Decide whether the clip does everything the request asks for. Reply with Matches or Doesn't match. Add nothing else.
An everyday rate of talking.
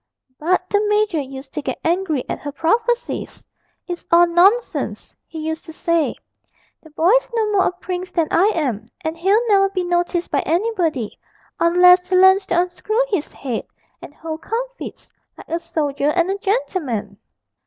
Matches